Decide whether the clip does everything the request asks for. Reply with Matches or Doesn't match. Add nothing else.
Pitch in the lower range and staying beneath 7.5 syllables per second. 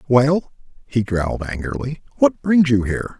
Matches